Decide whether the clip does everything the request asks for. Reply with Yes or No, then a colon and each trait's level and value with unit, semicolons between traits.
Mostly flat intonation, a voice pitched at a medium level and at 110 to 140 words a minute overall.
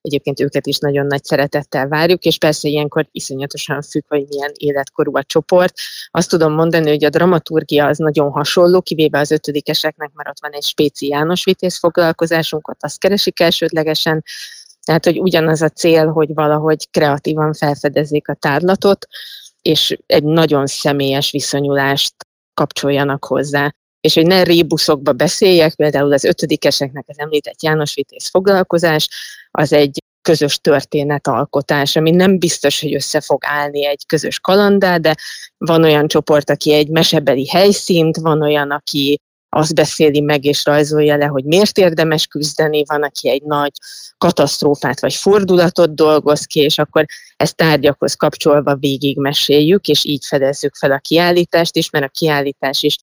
No: narrow, 2.1 semitones; medium, 150 Hz; average, 150 wpm